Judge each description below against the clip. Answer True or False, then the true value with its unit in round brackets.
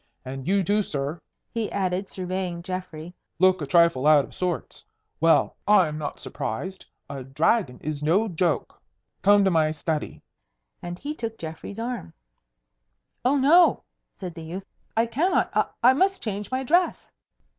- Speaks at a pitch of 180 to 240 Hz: True (185 Hz)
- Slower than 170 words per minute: True (155 wpm)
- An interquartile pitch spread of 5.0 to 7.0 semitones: True (5.5 semitones)